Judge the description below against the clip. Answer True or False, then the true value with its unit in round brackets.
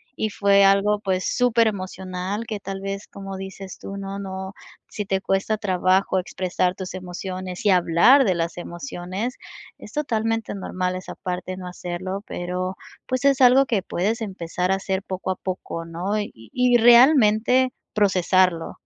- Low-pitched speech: False (195 Hz)